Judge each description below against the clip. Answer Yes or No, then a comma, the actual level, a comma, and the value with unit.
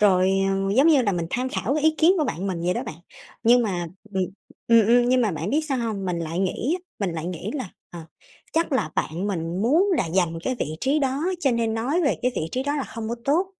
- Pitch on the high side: Yes, high, 225 Hz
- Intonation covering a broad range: Yes, wide, 6.9 semitones